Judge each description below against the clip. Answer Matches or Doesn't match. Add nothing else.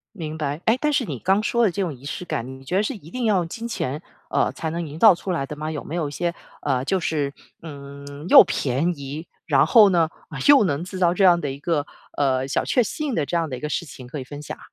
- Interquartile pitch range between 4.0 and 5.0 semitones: Matches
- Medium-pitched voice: Matches